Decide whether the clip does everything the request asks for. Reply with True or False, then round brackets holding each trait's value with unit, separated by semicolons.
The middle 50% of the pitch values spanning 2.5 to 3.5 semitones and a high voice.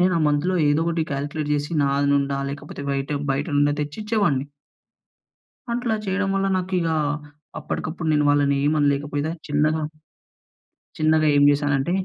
False (2.8 semitones; 150 Hz)